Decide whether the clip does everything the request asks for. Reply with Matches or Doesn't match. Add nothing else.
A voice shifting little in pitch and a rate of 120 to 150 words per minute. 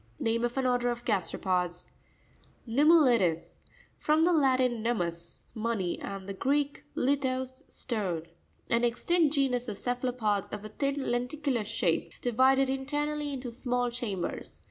Doesn't match